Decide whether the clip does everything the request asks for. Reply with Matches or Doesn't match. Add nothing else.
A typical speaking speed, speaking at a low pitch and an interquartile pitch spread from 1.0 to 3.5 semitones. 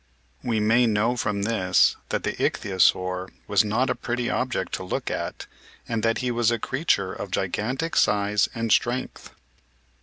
Matches